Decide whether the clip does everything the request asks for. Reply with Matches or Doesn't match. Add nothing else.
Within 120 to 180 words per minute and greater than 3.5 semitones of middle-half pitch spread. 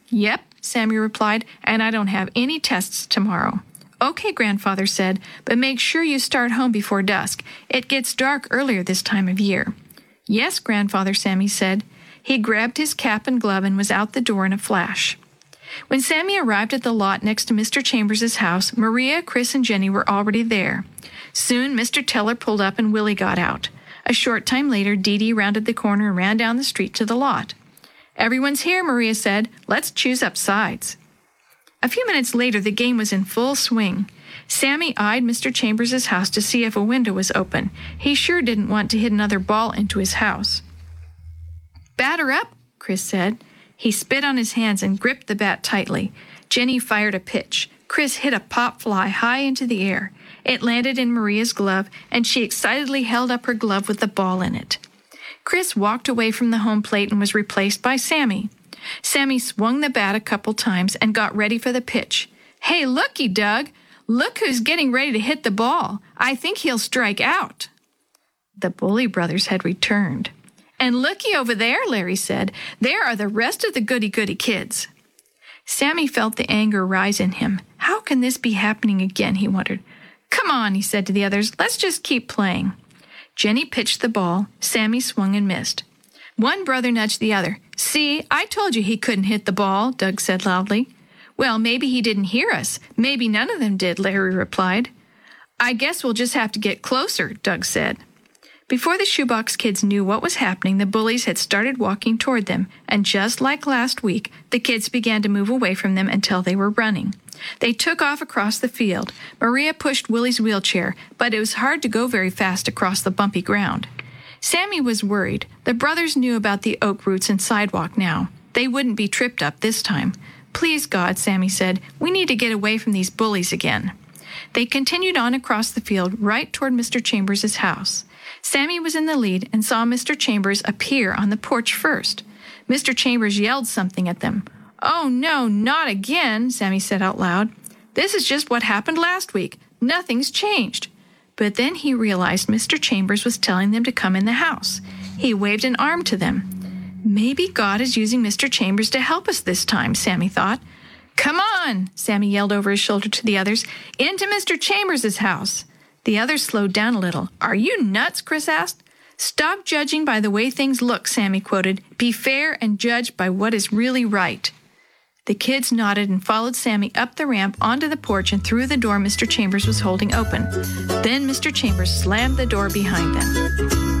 Doesn't match